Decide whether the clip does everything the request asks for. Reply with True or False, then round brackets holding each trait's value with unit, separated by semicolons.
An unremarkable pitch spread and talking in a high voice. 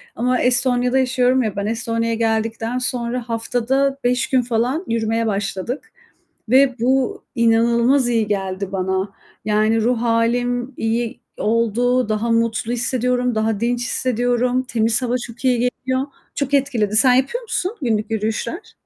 False (2.0 semitones; 235 Hz)